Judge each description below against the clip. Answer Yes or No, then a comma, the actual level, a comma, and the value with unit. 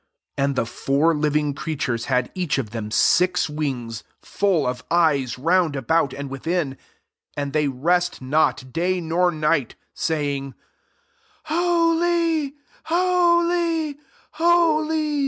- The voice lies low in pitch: No, medium, 160 Hz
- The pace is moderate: No, slow, 120 wpm